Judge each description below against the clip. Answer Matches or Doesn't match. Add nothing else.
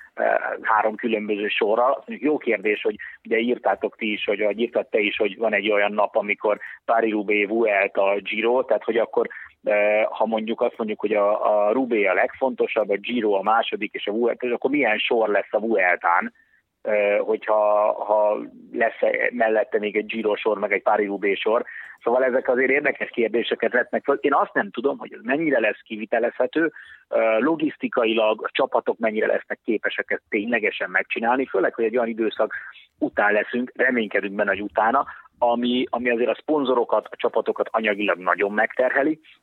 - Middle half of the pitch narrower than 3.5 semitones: Matches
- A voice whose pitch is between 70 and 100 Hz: Doesn't match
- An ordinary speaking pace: Doesn't match